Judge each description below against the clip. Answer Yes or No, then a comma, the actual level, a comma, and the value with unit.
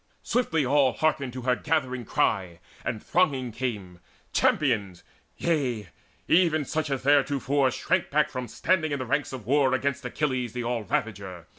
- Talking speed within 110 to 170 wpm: Yes, average, 150 wpm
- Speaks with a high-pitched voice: No, low, 130 Hz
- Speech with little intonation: No, average, 3.7 semitones